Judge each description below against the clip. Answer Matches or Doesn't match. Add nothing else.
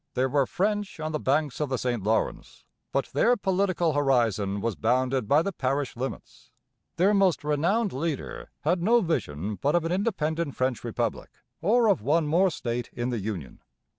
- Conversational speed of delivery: Matches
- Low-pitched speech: Doesn't match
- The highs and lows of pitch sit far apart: Matches